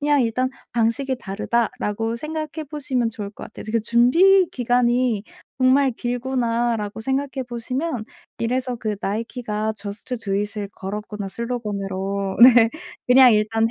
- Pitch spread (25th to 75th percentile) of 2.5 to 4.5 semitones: Yes, average, 3.4 semitones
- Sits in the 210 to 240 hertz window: Yes, high, 235 Hz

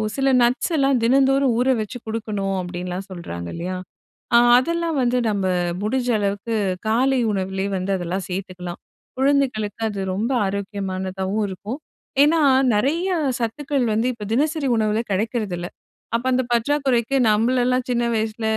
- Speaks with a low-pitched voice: No, high, 225 Hz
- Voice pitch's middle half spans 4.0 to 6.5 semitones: Yes, average, 5.2 semitones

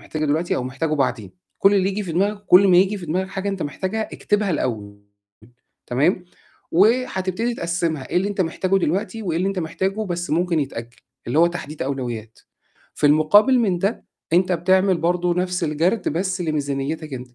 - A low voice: No, medium, 175 Hz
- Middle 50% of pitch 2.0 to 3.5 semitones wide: No, average, 4.1 semitones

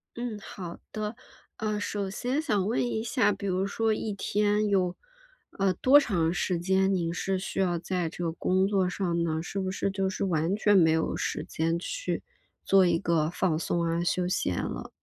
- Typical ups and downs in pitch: Yes, average, 3.2 semitones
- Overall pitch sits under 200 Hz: Yes, high, 190 Hz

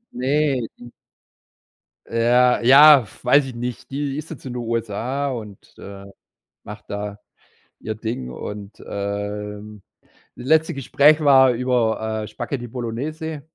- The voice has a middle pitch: No, low, 120 Hz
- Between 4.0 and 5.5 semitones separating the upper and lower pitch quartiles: Yes, average, 4.4 semitones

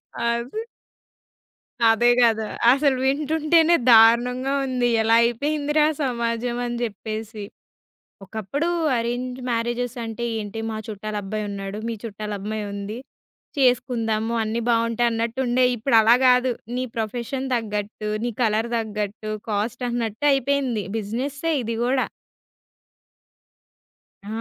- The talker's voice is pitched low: No, high, 235 Hz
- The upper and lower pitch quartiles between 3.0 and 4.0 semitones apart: No, narrow, 2.6 semitones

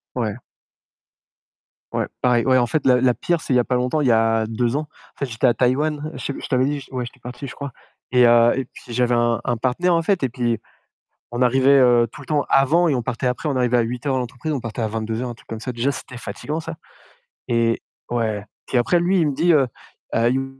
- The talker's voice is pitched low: Yes, low, 125 Hz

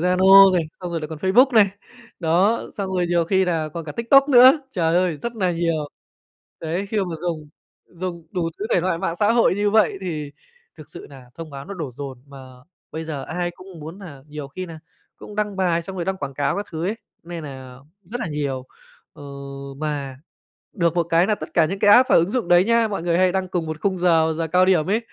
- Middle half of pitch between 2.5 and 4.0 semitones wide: Yes, average, 3.5 semitones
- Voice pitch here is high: No, medium, 175 Hz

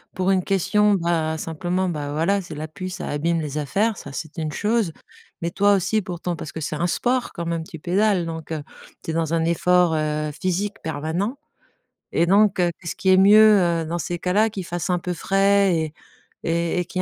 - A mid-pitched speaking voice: Yes, medium, 175 Hz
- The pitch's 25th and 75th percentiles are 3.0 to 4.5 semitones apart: Yes, average, 3.3 semitones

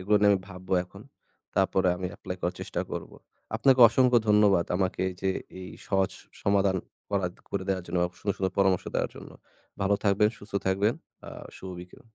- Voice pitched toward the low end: Yes, very low, 95 Hz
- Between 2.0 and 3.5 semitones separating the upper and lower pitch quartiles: No, narrow, 1.6 semitones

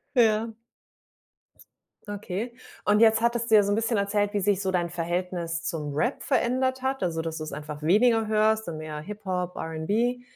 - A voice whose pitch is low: No, high, 205 Hz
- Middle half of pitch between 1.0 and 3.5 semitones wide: No, average, 5.0 semitones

